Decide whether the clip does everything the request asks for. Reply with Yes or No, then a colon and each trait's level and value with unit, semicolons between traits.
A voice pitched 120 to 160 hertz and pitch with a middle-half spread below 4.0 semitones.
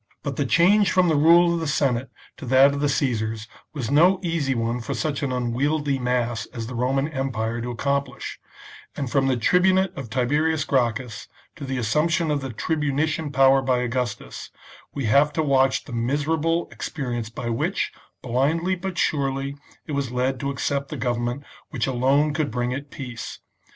Yes: low, 135 Hz; average, 3.5 semitones